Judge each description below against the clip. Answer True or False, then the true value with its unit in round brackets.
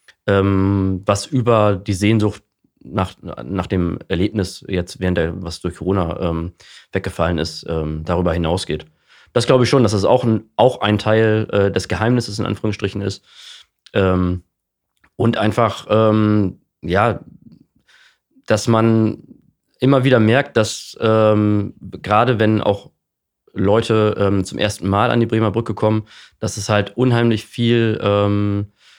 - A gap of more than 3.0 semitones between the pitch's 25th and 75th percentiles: False (2.7 semitones)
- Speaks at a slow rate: False (145 wpm)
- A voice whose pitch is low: True (105 Hz)